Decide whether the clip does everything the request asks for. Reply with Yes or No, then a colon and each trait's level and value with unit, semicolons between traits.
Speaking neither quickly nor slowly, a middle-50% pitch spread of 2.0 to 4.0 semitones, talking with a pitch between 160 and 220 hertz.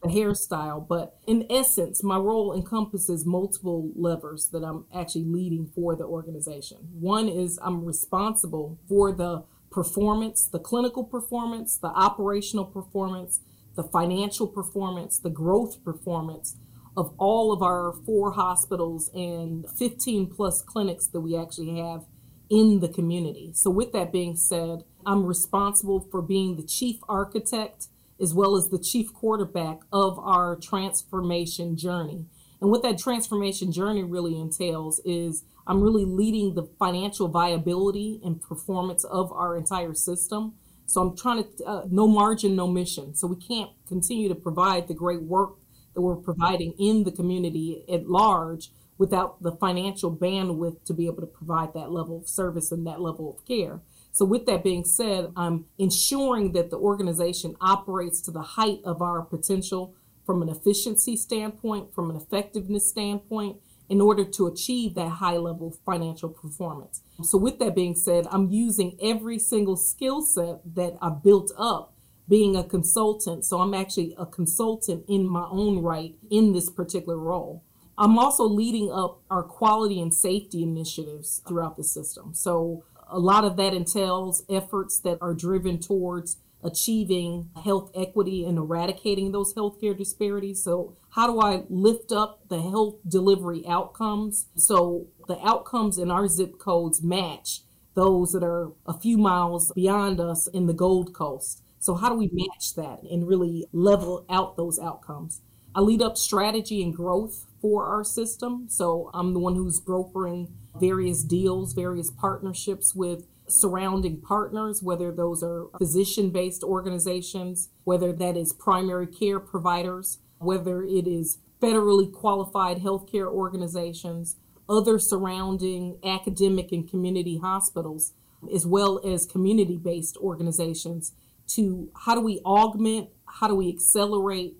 Yes: average, 150 wpm; average, 2.8 semitones; medium, 185 Hz